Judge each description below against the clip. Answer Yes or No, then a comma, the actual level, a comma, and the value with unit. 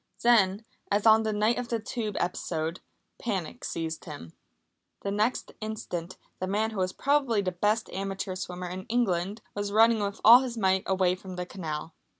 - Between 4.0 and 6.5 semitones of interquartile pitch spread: No, average, 3.3 semitones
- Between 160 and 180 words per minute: Yes, average, 175 wpm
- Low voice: No, high, 200 Hz